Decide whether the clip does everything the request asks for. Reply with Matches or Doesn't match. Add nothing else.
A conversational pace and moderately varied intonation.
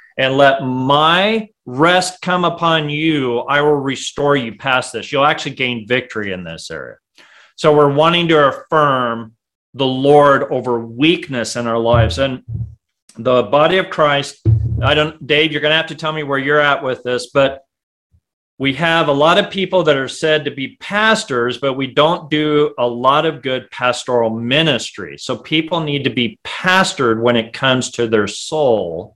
Matches